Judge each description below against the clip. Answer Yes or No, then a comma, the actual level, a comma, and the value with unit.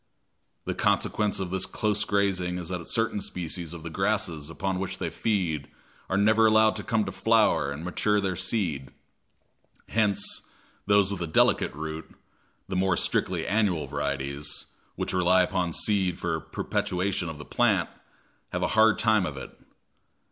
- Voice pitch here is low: Yes, very low, 95 Hz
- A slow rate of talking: No, average, 160 wpm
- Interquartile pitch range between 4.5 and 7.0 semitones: No, average, 3.9 semitones